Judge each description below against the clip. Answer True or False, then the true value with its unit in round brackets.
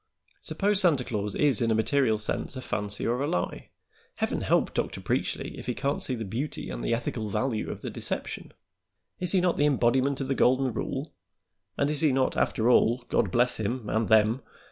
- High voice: False (125 Hz)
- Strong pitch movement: False (4.0 semitones)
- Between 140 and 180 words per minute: False (205 wpm)